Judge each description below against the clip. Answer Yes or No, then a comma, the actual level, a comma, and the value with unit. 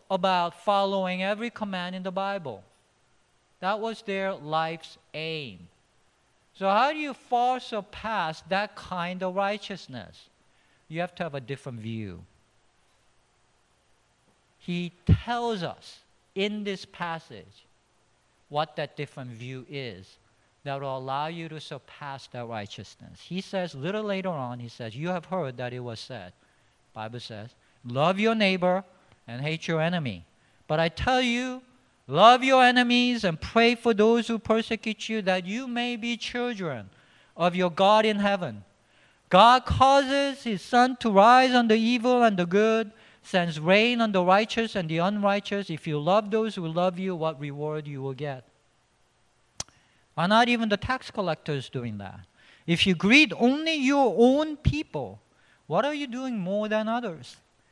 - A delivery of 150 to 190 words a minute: Yes, average, 155 wpm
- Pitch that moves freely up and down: Yes, wide, 8.4 semitones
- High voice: No, medium, 180 Hz